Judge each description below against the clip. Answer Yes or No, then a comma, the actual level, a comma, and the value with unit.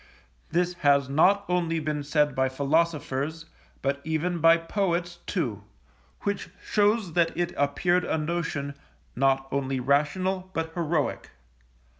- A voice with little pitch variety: No, average, 3.7 semitones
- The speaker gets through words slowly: Yes, slow, 125 wpm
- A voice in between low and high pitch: Yes, medium, 160 Hz